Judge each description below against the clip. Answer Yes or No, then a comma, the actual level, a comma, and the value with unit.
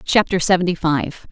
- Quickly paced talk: No, slow, 135 wpm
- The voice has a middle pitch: Yes, medium, 170 Hz